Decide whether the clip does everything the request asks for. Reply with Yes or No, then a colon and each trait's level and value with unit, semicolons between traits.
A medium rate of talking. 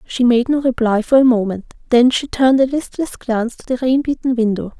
No: fast, 225 wpm